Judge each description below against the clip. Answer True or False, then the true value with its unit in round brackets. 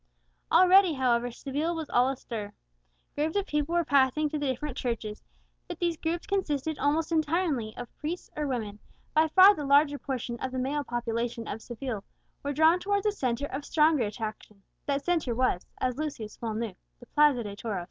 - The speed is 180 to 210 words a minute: True (185 wpm)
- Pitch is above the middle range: True (280 Hz)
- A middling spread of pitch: True (4.9 semitones)